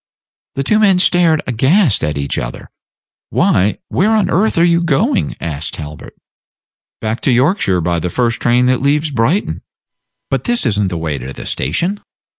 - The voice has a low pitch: Yes, low, 130 Hz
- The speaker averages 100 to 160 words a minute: No, average, 175 wpm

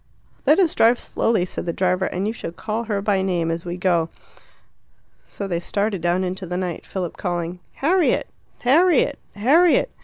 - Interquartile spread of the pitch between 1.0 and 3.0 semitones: No, average, 4.5 semitones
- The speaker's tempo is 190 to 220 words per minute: No, average, 175 wpm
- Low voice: No, high, 190 Hz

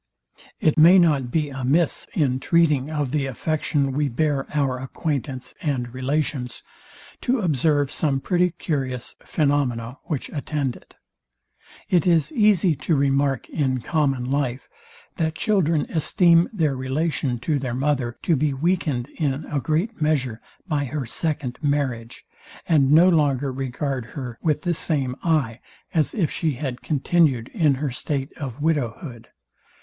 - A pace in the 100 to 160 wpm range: Yes, average, 145 wpm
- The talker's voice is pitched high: No, medium, 145 Hz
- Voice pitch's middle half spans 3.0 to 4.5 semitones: Yes, average, 3.3 semitones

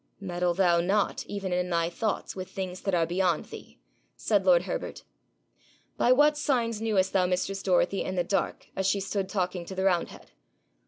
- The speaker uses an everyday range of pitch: No, narrow, 2.0 semitones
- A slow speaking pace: No, average, 180 wpm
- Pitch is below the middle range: No, high, 190 Hz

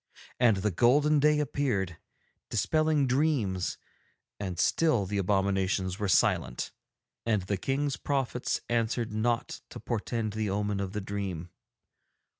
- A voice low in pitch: Yes, low, 105 Hz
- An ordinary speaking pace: No, slow, 125 wpm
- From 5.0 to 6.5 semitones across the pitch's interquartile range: Yes, wide, 5.5 semitones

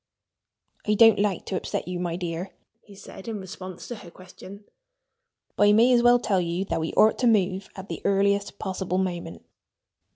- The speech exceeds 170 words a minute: Yes, average, 190 wpm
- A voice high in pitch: Yes, high, 195 Hz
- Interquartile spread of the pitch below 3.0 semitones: Yes, narrow, 2.5 semitones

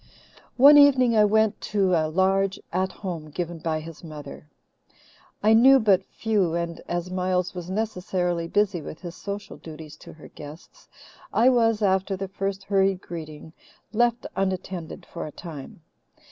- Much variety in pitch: No, average, 3.6 semitones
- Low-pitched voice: No, medium, 185 Hz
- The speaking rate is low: No, average, 155 wpm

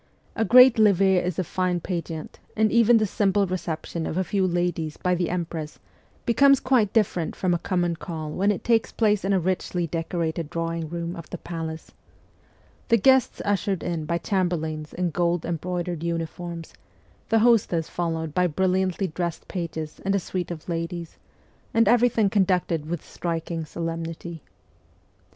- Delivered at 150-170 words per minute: Yes, average, 160 wpm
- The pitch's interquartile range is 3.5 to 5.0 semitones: No, average, 2.7 semitones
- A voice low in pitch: No, medium, 175 Hz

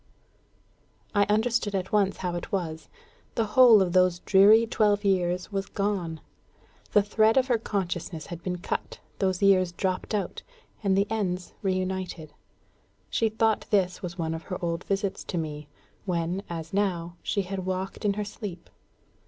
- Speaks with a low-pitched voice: No, high, 190 Hz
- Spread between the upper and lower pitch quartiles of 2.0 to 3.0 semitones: Yes, average, 2.7 semitones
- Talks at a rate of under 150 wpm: No, average, 160 wpm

